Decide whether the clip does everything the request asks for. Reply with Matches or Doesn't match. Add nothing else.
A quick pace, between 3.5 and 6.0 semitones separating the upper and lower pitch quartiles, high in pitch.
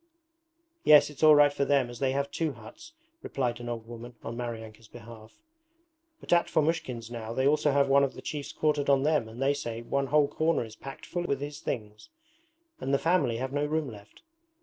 Doesn't match